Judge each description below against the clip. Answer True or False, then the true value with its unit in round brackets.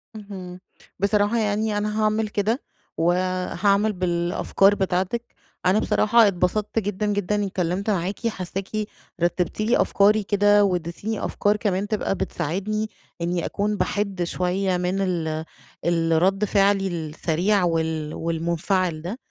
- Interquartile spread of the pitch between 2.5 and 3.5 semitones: True (2.9 semitones)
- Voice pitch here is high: True (195 Hz)